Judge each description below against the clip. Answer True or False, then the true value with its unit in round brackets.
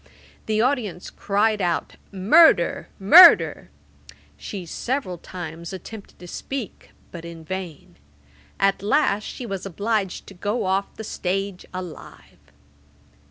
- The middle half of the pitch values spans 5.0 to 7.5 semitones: False (3.5 semitones)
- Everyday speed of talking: False (115 wpm)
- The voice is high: True (195 Hz)